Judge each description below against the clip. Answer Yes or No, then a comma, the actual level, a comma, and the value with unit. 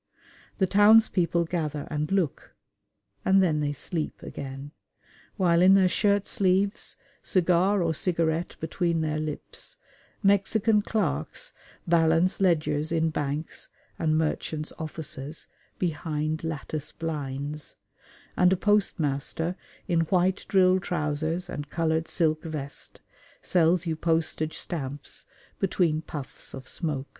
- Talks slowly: Yes, slow, 115 wpm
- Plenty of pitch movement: No, average, 3.1 semitones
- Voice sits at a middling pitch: Yes, medium, 165 Hz